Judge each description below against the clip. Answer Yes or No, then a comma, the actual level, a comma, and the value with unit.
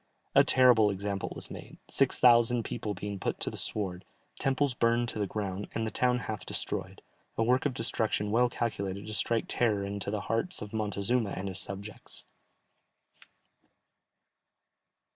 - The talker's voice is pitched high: No, low, 110 Hz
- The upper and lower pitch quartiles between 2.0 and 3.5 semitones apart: Yes, average, 3.0 semitones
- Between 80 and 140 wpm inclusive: No, average, 160 wpm